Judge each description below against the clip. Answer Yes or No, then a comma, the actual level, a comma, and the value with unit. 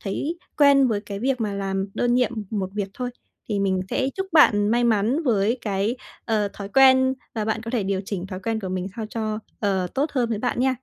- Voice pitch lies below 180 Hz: No, high, 220 Hz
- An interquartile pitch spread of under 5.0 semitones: Yes, average, 4.1 semitones